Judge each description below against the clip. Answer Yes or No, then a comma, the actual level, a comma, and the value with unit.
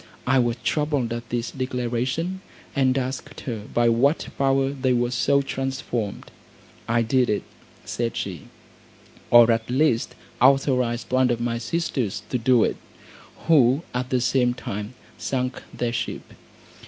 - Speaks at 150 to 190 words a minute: No, average, 140 wpm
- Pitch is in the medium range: No, low, 125 Hz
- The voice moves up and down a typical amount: No, narrow, 2.2 semitones